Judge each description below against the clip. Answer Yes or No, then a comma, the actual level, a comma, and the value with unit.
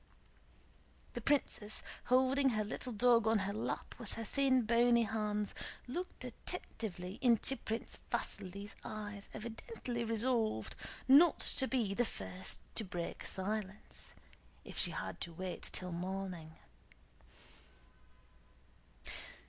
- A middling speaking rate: No, slow, 115 wpm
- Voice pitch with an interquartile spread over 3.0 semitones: Yes, average, 3.9 semitones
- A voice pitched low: No, high, 220 Hz